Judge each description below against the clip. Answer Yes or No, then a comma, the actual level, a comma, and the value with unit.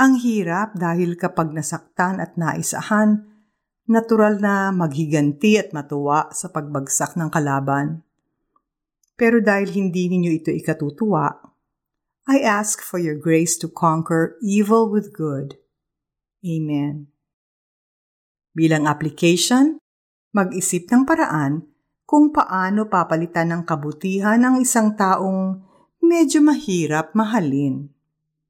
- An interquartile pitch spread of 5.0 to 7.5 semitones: Yes, wide, 5.4 semitones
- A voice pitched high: No, medium, 175 Hz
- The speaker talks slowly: Yes, slow, 105 wpm